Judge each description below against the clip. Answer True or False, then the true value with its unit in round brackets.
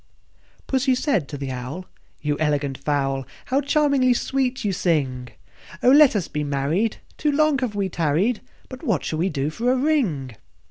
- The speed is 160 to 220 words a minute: True (180 wpm)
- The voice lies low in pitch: False (185 Hz)